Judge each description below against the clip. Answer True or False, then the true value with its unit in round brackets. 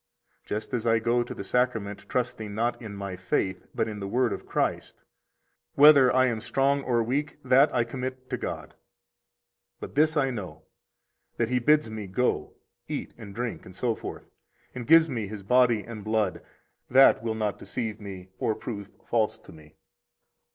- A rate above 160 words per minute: True (170 wpm)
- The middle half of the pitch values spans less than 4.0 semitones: True (3.6 semitones)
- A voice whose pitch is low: True (115 Hz)